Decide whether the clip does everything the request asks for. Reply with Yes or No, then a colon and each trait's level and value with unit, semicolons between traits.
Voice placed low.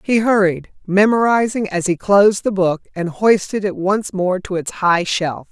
No: high, 195 Hz